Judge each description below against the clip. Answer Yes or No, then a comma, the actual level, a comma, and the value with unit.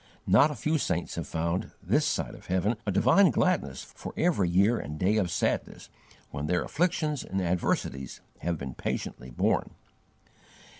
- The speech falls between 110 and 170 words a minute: Yes, average, 160 wpm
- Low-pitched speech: Yes, very low, 95 Hz